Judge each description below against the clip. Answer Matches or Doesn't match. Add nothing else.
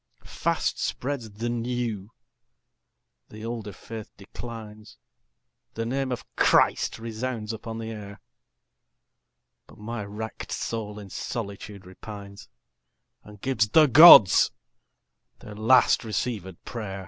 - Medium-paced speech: Doesn't match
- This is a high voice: Doesn't match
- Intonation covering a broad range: Doesn't match